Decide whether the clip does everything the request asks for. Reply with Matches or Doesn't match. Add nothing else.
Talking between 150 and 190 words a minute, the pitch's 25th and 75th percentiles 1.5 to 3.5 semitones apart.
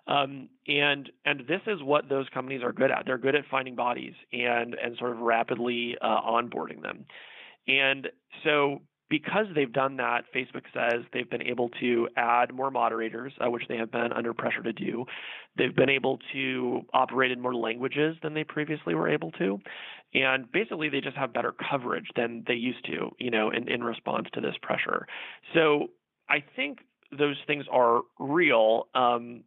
Matches